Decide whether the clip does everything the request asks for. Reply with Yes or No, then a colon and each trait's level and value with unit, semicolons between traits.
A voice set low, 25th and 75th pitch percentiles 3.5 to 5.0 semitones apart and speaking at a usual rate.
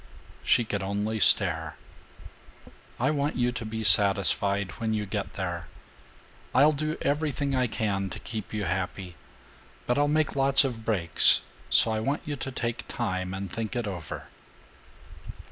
No: low, 110 Hz; wide, 5.4 semitones; average, 155 wpm